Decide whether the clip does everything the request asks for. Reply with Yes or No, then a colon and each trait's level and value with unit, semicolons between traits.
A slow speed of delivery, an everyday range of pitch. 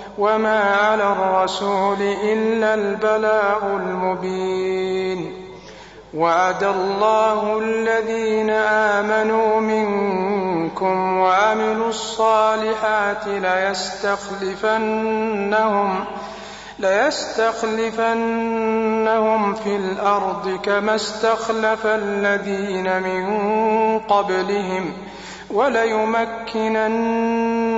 No: slow, 50 wpm; narrow, 2.1 semitones